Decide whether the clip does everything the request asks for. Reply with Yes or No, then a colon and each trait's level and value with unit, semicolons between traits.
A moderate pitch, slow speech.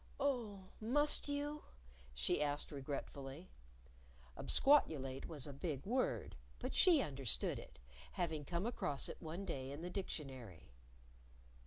Yes: medium, 160 Hz; slow, 125 wpm